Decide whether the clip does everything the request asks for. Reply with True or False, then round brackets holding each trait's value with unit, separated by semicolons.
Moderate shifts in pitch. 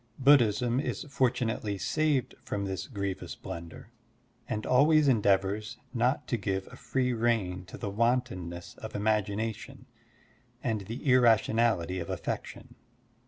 True (4.2 semitones)